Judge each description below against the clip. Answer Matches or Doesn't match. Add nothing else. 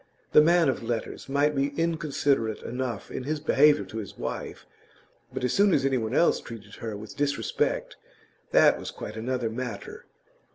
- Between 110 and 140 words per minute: Doesn't match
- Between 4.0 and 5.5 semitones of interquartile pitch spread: Matches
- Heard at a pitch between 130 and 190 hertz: Matches